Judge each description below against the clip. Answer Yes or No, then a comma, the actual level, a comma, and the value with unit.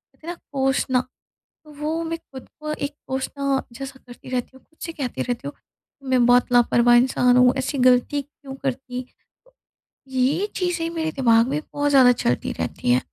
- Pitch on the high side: Yes, very high, 265 Hz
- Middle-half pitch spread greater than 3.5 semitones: No, average, 2.7 semitones